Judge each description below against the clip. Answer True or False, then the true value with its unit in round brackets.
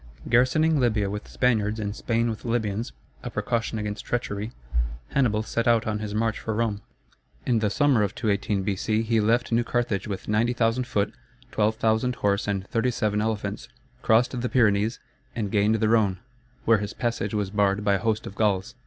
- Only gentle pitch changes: True (2.1 semitones)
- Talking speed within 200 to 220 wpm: False (175 wpm)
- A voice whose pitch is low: True (110 Hz)